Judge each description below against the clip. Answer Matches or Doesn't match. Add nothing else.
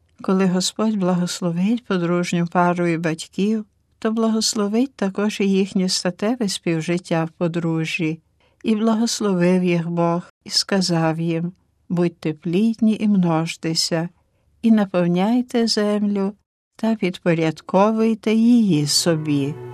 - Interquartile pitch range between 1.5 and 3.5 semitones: Doesn't match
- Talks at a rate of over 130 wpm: Doesn't match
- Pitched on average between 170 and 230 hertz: Matches